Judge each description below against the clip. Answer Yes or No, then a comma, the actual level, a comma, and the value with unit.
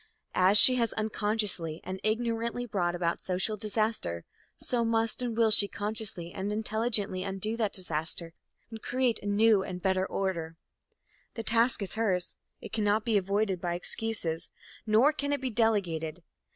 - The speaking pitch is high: Yes, high, 210 Hz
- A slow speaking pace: No, average, 160 wpm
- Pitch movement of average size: Yes, average, 3.4 semitones